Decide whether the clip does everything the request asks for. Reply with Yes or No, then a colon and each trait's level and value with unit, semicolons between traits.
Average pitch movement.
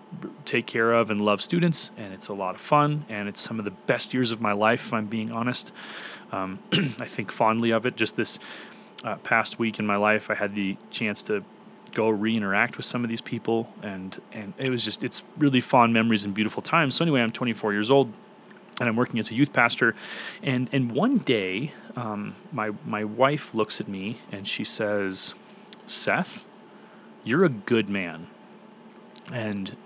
Yes: average, 3.1 semitones